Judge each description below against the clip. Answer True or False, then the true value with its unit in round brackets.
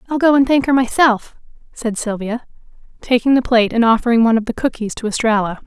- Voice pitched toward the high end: True (235 Hz)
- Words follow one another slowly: False (200 wpm)